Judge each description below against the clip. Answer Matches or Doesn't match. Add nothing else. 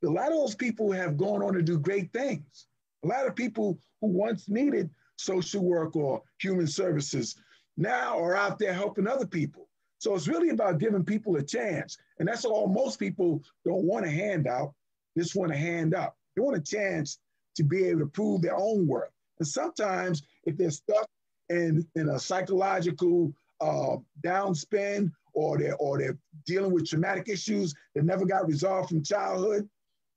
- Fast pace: Matches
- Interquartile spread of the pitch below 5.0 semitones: Matches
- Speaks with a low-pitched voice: Doesn't match